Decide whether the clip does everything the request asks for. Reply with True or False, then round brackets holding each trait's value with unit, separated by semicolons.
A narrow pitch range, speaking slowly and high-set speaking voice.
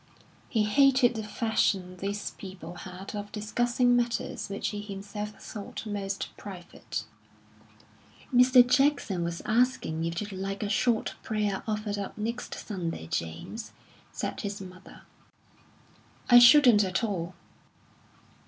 False (3.5 semitones; 125 wpm; 205 Hz)